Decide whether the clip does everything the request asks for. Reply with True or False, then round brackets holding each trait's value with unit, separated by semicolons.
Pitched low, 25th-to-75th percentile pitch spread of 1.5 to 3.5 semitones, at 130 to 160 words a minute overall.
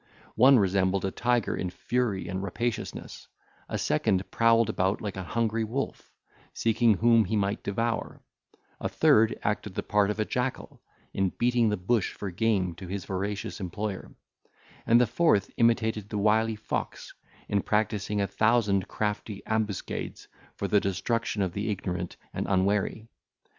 True (105 Hz; 2.7 semitones; 155 wpm)